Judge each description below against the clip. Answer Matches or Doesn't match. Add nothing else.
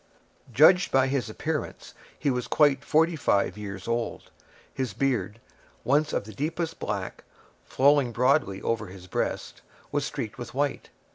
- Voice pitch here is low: Matches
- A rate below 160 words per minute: Matches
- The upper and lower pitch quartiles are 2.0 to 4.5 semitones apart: Doesn't match